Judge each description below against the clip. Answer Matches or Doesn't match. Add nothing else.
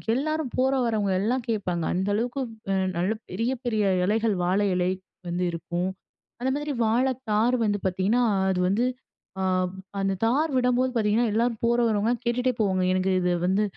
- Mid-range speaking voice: Doesn't match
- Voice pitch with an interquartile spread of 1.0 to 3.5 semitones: Doesn't match